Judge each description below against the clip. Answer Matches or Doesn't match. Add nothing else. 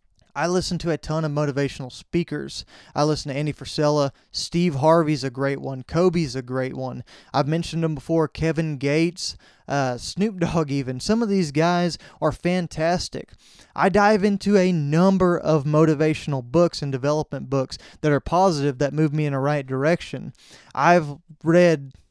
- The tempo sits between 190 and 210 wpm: Doesn't match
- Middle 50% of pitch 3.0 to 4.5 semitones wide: Matches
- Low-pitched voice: Doesn't match